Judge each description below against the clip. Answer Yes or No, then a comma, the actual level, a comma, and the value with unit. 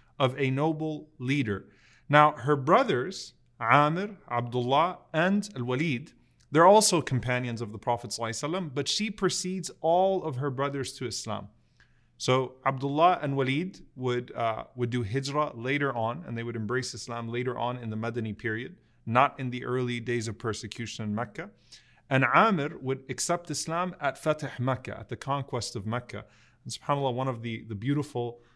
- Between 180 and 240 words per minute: No, average, 165 wpm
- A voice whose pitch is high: No, low, 130 Hz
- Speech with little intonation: No, average, 3.6 semitones